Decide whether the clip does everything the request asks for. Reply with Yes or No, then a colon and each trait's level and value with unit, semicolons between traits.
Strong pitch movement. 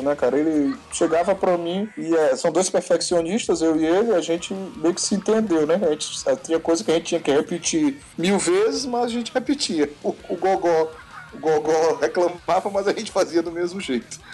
No: average, 3.6 semitones